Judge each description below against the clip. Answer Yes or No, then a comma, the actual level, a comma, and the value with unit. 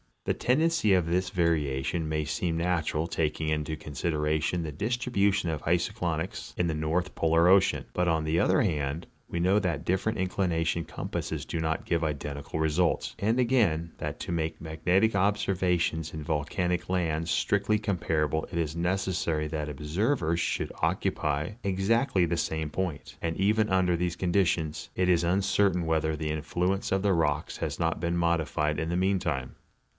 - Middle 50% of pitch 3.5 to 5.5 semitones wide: No, average, 3.0 semitones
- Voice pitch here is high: No, very low, 85 Hz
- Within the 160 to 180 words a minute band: Yes, average, 165 wpm